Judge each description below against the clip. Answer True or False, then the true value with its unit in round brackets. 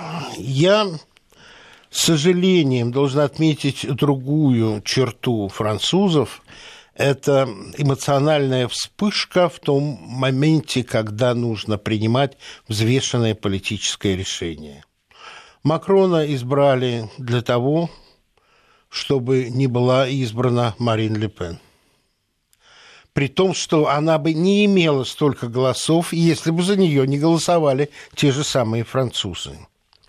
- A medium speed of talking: False (100 wpm)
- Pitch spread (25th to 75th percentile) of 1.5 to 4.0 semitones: False (4.9 semitones)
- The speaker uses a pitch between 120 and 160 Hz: True (135 Hz)